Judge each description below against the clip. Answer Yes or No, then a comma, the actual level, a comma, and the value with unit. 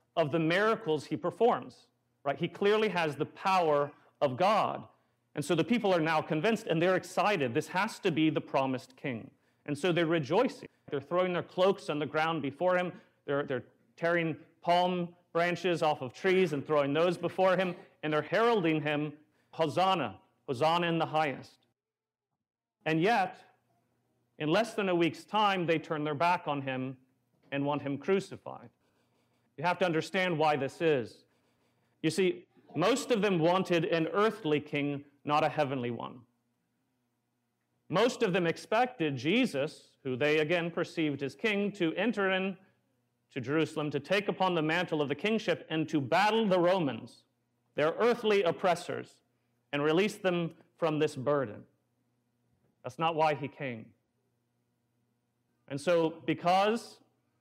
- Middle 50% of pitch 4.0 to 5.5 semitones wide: Yes, average, 4.7 semitones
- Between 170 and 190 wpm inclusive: No, average, 155 wpm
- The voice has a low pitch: No, medium, 155 Hz